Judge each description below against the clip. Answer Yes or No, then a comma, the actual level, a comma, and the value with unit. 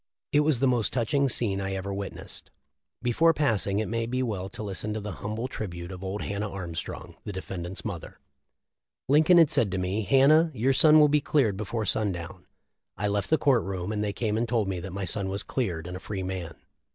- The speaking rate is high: Yes, fast, 225 wpm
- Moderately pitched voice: No, low, 105 Hz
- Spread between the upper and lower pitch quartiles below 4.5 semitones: No, average, 4.8 semitones